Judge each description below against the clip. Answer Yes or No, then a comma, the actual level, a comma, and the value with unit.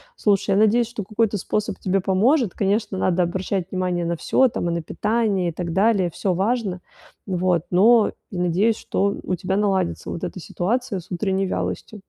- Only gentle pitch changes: No, average, 3.0 semitones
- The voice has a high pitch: Yes, high, 195 Hz